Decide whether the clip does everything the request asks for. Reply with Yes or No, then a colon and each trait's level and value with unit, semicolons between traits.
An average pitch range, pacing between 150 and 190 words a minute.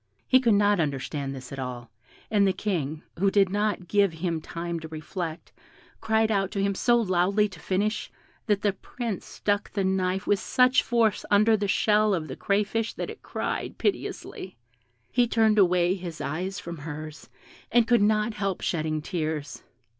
Yes: average, 4.3 semitones; average, 175 wpm